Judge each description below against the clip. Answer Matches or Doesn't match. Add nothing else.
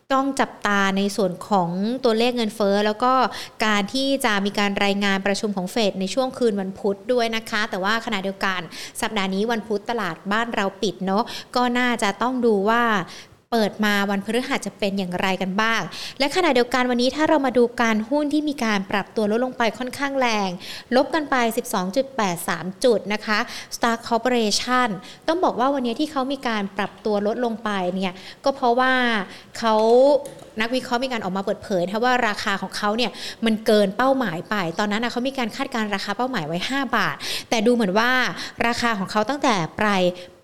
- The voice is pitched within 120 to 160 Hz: Doesn't match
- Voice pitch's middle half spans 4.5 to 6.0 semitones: Doesn't match